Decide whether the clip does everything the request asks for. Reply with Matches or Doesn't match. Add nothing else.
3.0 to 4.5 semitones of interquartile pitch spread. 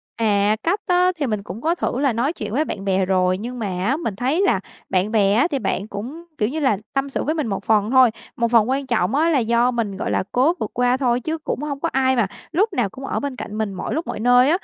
Doesn't match